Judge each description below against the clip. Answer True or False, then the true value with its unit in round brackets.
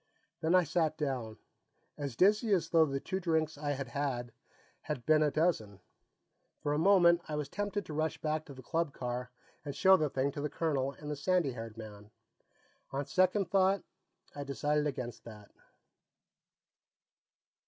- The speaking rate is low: False (170 wpm)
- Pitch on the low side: False (150 Hz)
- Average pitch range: True (3.9 semitones)